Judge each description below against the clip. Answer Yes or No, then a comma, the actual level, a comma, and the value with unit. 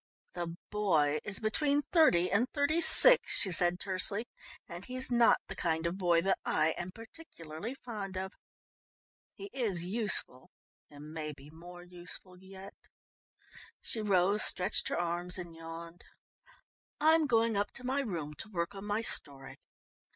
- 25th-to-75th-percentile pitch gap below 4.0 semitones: No, average, 5.0 semitones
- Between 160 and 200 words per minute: No, average, 150 wpm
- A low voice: No, high, 190 Hz